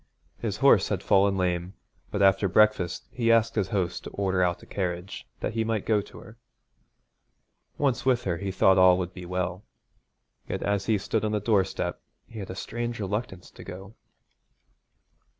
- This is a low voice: Yes, low, 100 Hz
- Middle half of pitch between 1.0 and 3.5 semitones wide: Yes, average, 3.0 semitones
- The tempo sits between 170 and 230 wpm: Yes, average, 180 wpm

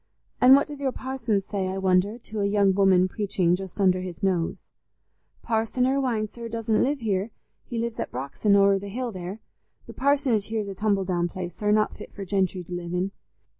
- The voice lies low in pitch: No, high, 200 Hz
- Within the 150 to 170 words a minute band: No, fast, 205 wpm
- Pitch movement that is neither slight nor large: Yes, average, 3.6 semitones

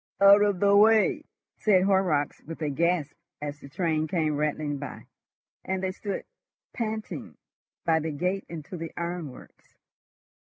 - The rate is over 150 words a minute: No, average, 140 wpm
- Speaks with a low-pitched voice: No, medium, 170 Hz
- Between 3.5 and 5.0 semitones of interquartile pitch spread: Yes, average, 4.3 semitones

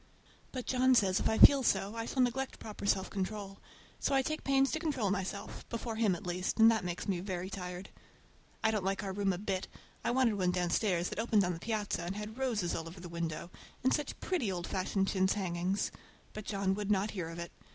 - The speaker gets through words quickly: Yes, fast, 220 wpm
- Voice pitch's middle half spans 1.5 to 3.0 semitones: No, average, 3.7 semitones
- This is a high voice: Yes, high, 200 Hz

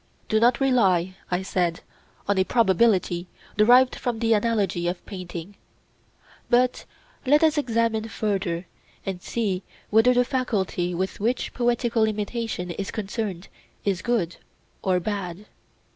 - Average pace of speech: No, slow, 130 wpm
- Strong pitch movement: No, average, 4.3 semitones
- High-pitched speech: Yes, high, 210 Hz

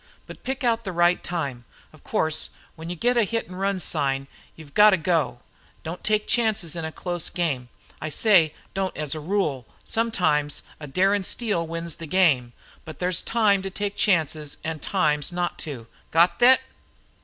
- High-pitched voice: No, medium, 175 Hz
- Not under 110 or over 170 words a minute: No, average, 185 wpm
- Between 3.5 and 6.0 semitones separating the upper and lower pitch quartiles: Yes, average, 4.5 semitones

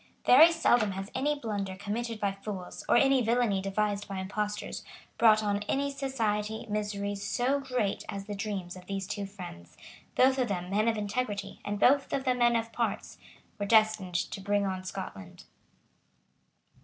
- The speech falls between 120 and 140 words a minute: No, average, 170 wpm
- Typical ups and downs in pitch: Yes, average, 3.3 semitones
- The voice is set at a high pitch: Yes, high, 210 Hz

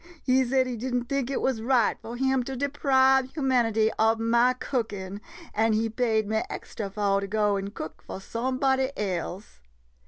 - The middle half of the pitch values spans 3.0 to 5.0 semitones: Yes, average, 3.5 semitones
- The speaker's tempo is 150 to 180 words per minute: No, average, 190 wpm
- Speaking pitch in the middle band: No, high, 235 Hz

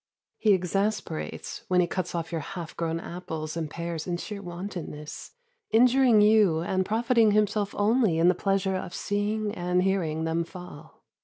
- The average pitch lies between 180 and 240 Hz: Yes, medium, 185 Hz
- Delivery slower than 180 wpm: Yes, average, 160 wpm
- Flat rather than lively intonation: No, average, 3.7 semitones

